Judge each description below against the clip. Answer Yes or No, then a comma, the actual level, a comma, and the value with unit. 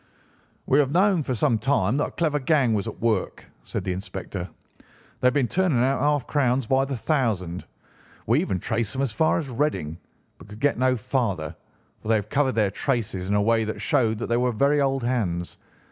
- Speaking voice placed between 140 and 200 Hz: No, low, 120 Hz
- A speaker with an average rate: No, fast, 210 wpm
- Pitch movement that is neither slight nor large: Yes, average, 4.9 semitones